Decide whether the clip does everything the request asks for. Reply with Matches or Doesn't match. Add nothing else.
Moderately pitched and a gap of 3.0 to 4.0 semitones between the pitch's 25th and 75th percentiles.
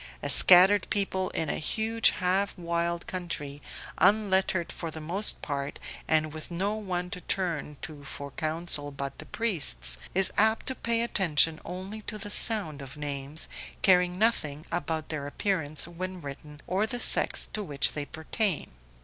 Doesn't match